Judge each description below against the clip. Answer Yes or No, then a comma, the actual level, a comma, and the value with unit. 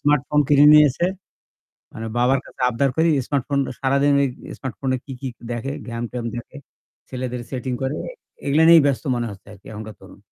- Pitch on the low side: Yes, low, 130 Hz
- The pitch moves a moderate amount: Yes, average, 3.1 semitones